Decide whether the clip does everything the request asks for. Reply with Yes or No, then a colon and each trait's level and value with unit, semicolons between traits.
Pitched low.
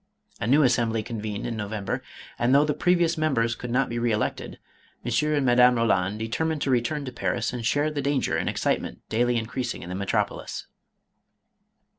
Yes: low, 120 Hz